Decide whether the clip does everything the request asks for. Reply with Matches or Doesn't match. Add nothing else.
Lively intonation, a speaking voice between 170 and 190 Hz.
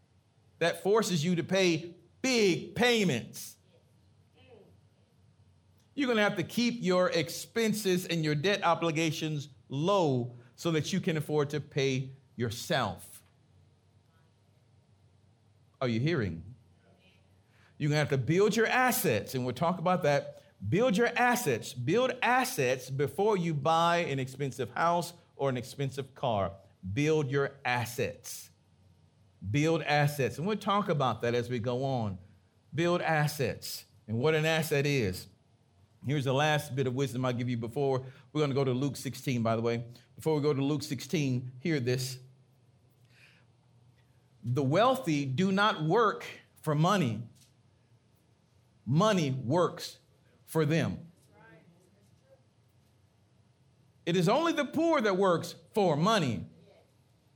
Doesn't match